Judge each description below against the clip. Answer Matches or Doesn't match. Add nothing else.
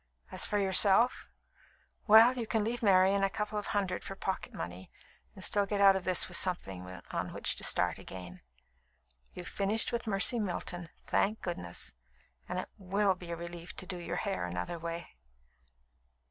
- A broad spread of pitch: Doesn't match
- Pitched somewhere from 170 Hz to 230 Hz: Matches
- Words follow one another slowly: Doesn't match